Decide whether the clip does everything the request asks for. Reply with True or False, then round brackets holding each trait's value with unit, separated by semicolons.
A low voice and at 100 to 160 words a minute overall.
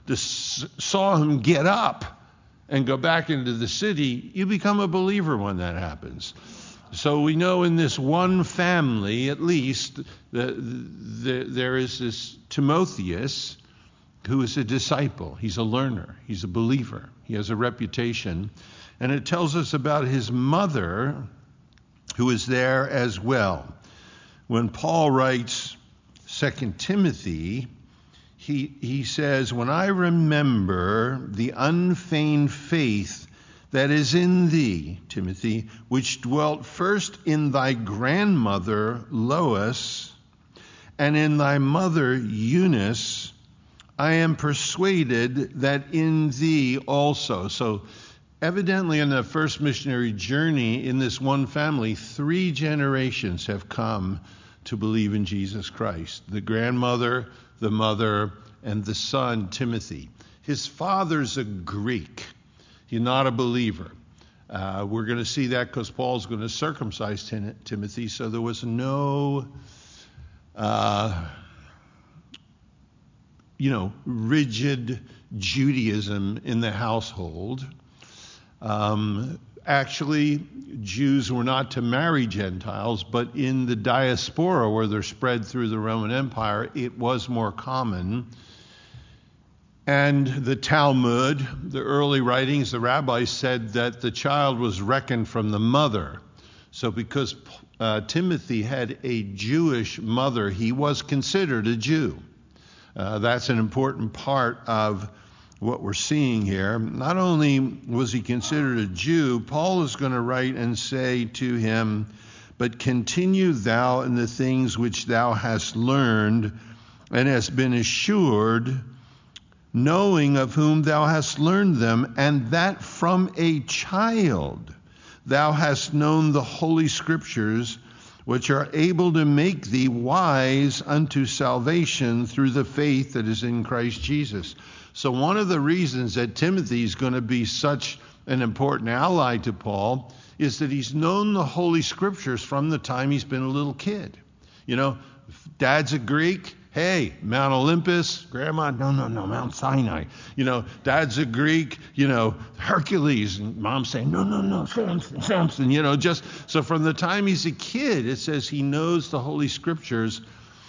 True (130 Hz; 135 wpm)